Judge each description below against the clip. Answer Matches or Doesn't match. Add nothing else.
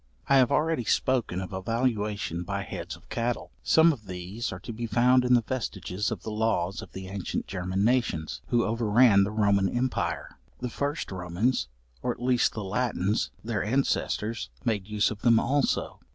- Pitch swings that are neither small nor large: Matches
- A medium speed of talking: Matches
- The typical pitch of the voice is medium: Doesn't match